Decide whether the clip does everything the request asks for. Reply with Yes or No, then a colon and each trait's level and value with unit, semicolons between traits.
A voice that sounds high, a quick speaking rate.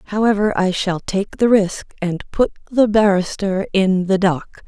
No: high, 195 Hz; average, 165 wpm